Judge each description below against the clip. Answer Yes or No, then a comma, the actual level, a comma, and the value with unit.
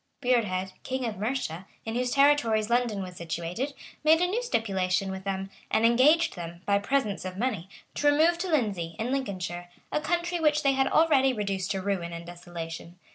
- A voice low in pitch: No, high, 220 Hz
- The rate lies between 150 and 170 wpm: No, average, 185 wpm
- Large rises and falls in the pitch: Yes, wide, 6.9 semitones